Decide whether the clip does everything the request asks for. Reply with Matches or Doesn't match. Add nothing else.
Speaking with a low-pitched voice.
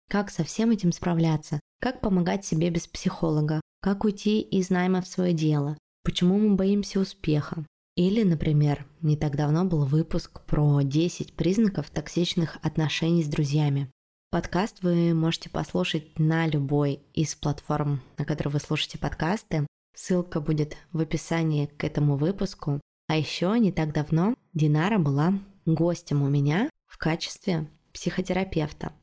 Doesn't match